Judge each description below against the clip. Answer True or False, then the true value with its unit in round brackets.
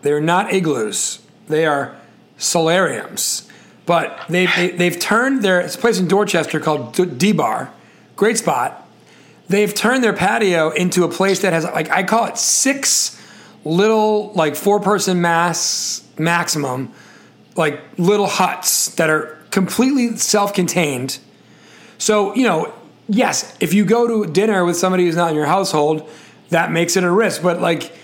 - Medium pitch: True (180 Hz)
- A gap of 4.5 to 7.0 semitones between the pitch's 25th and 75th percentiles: False (3.9 semitones)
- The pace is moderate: True (160 wpm)